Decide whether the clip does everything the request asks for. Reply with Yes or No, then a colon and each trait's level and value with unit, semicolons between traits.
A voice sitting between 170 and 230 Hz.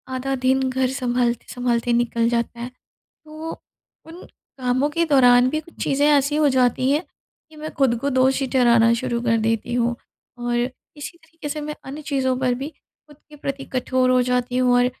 No: very high, 255 Hz